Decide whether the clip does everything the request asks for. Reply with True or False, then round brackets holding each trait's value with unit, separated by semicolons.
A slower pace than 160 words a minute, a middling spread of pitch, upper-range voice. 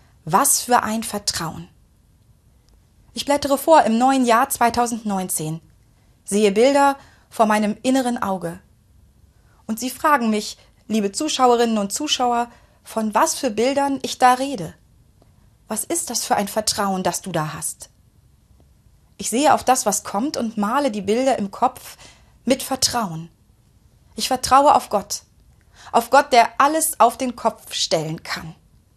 True (145 wpm; 5.0 semitones; 225 Hz)